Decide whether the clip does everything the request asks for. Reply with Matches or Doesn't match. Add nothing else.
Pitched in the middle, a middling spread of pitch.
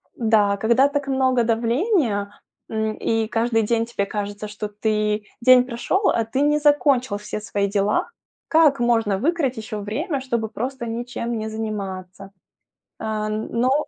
Doesn't match